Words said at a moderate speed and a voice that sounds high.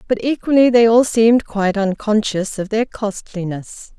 Yes: average, 150 wpm; high, 220 Hz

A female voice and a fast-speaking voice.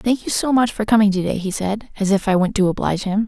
Yes: female; fast, 275 wpm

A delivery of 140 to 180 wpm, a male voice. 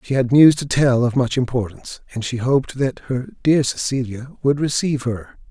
No: average, 195 wpm; male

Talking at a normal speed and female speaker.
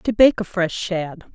No: fast, 225 wpm; female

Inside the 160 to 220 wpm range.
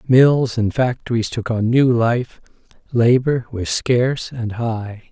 No: average, 140 wpm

